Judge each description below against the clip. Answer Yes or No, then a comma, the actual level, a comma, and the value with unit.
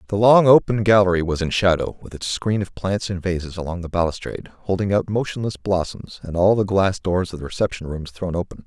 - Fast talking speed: Yes, fast, 220 wpm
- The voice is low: Yes, very low, 95 Hz